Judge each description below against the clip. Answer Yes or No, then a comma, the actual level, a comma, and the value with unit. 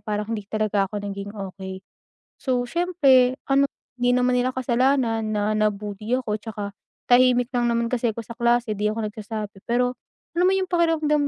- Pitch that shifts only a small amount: No, average, 3.3 semitones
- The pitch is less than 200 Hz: No, high, 235 Hz